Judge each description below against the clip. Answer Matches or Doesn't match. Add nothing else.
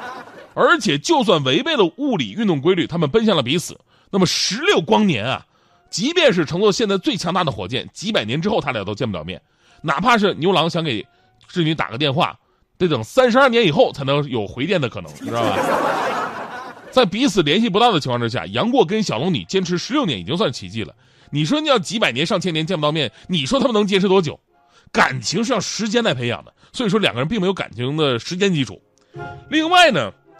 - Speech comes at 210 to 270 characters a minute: Doesn't match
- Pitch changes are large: Matches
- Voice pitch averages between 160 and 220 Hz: Matches